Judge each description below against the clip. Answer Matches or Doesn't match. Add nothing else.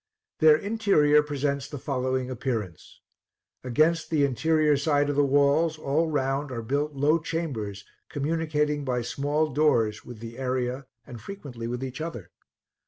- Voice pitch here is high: Doesn't match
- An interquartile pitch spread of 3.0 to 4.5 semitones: Matches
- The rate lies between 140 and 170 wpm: Matches